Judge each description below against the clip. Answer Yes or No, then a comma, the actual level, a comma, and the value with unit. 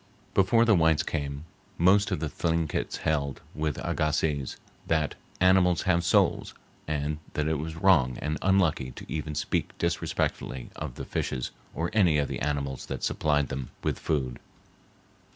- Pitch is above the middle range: No, very low, 75 Hz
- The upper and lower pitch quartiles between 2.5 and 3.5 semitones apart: Yes, average, 2.9 semitones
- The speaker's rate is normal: Yes, average, 150 wpm